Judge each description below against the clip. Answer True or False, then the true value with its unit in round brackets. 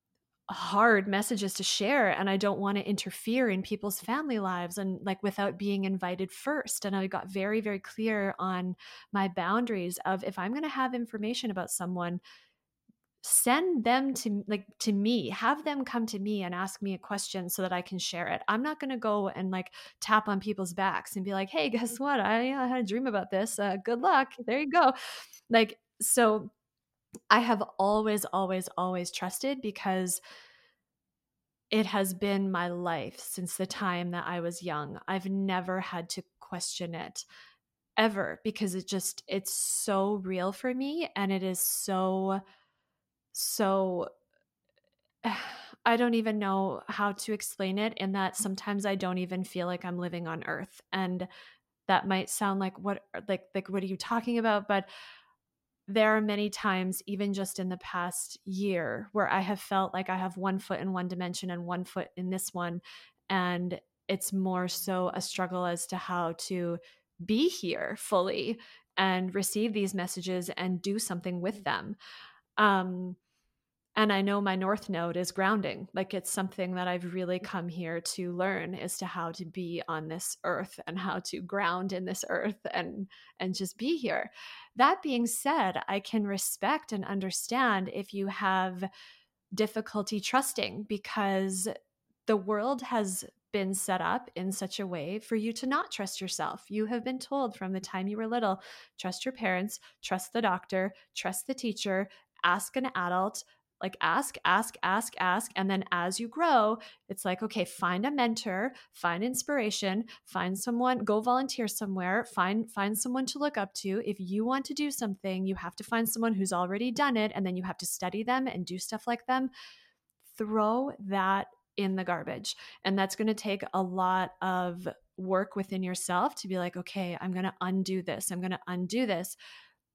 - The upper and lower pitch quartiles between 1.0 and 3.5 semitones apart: True (2.9 semitones)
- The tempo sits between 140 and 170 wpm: False (180 wpm)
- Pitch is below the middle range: False (195 Hz)